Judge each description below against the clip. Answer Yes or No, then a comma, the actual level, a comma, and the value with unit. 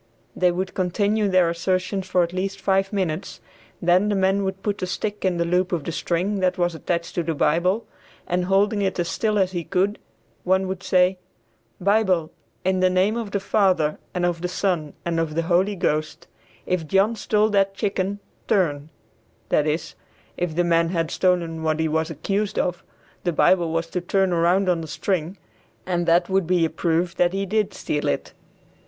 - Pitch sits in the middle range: Yes, medium, 180 Hz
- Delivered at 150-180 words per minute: No, average, 195 wpm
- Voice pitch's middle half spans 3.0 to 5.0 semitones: No, narrow, 2.4 semitones